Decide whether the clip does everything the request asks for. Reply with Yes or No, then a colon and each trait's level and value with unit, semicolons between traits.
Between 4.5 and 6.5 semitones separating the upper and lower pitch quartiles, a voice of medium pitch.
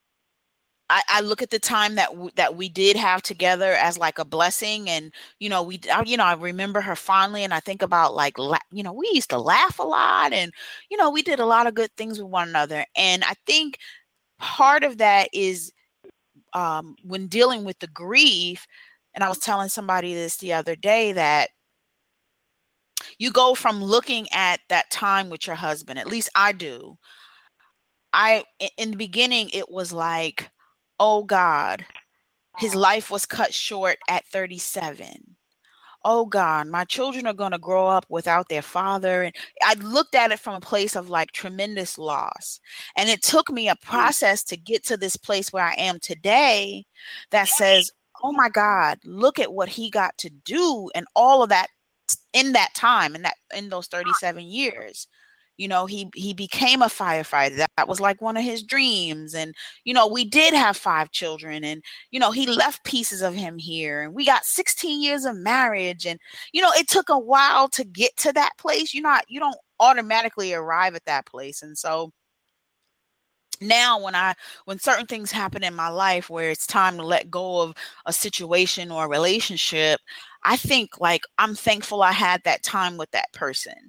No: average, 4.8 semitones; high, 195 Hz